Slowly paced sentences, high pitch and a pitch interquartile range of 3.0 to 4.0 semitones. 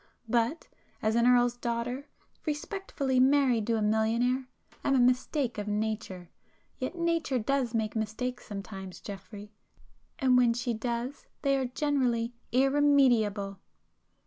Yes: slow, 125 wpm; high, 245 Hz; average, 3.5 semitones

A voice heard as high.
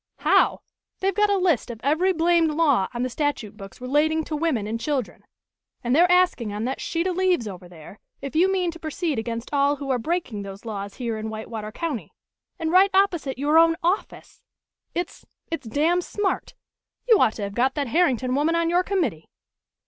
Yes: very high, 290 Hz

